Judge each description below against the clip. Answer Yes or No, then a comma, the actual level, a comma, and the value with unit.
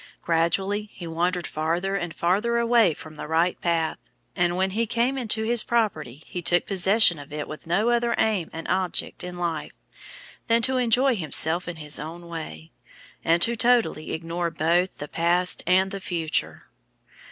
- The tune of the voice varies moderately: Yes, average, 4.8 semitones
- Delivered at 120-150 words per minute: No, average, 165 wpm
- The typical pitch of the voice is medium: Yes, medium, 175 Hz